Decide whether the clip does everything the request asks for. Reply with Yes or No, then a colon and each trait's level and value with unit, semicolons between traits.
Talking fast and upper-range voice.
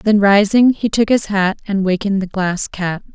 Yes: fast, 210 wpm; high, 200 Hz